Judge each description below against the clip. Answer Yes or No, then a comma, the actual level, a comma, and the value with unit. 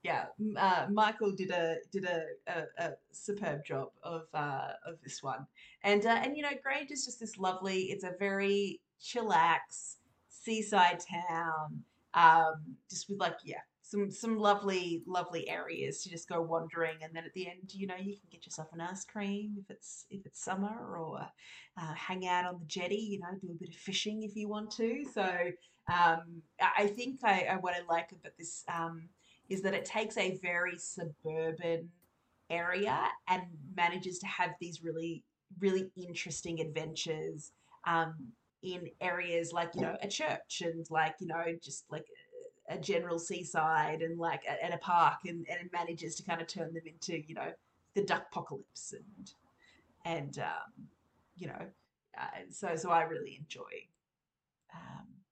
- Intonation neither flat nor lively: Yes, average, 3.2 semitones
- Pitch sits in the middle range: Yes, medium, 180 Hz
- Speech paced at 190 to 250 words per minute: No, average, 175 wpm